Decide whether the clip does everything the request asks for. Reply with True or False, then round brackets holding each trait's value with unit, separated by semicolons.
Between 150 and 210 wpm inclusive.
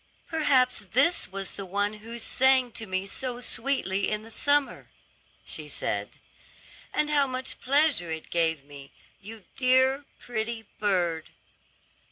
False (135 wpm)